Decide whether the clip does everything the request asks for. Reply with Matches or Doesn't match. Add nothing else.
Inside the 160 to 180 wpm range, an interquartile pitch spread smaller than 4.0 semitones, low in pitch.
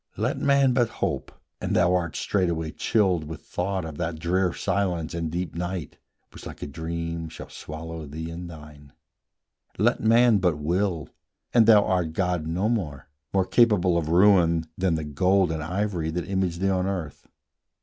Matches